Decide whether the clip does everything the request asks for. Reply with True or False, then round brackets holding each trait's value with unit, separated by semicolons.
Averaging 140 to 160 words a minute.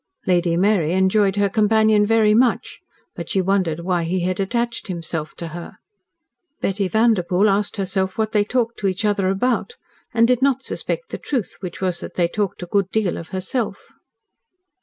False (180 wpm)